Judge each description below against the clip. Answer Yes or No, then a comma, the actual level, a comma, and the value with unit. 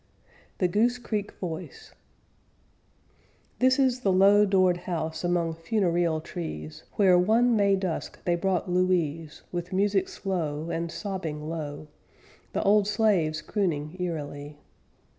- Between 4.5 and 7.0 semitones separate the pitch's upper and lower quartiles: No, average, 3.9 semitones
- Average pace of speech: No, slow, 120 wpm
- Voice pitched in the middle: Yes, medium, 180 Hz